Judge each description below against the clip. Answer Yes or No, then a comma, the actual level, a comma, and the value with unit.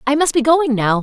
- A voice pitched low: No, very high, 270 Hz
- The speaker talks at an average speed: No, fast, 290 wpm